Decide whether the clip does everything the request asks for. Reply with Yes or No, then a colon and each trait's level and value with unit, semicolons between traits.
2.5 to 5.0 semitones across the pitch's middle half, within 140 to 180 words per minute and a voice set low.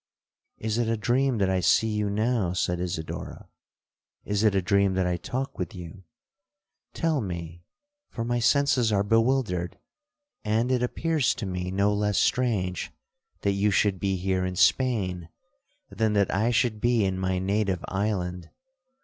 Yes: average, 4.1 semitones; average, 155 wpm; low, 100 Hz